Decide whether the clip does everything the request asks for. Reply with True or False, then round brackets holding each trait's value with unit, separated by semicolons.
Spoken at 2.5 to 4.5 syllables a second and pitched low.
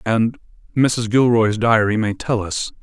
True (4.0 syllables/s; 110 Hz)